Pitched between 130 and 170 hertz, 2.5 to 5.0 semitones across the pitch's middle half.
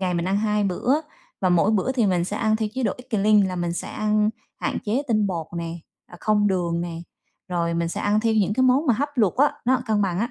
No: high, 210 Hz; average, 3.8 semitones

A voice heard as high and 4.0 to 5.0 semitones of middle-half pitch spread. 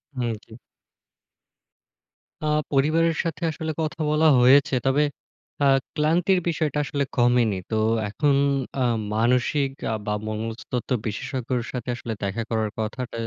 No: low, 130 Hz; average, 4.7 semitones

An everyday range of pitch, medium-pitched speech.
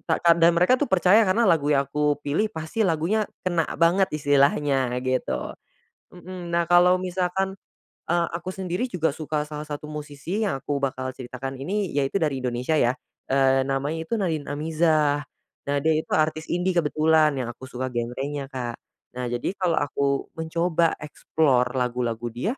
Yes: average, 4.3 semitones; medium, 155 Hz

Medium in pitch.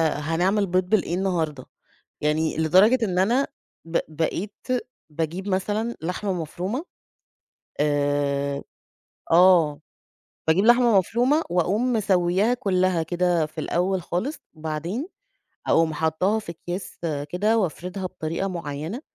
Yes: medium, 180 Hz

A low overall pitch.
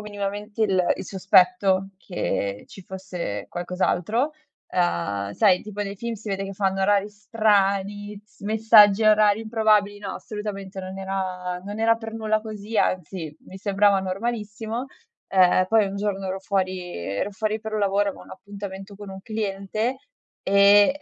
No: high, 200 Hz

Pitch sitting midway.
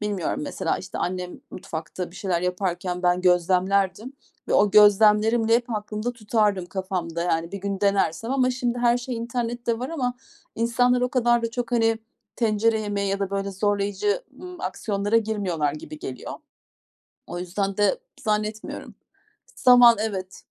No: high, 210 Hz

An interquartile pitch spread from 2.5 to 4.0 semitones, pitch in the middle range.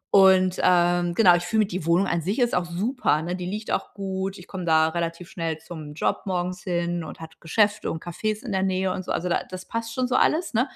Yes: average, 2.8 semitones; medium, 180 Hz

